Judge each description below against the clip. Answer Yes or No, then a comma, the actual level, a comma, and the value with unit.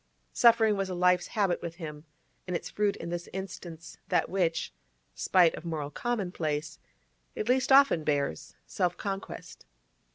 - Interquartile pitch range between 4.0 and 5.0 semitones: No, average, 3.5 semitones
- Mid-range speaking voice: Yes, medium, 180 Hz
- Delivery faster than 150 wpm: No, average, 140 wpm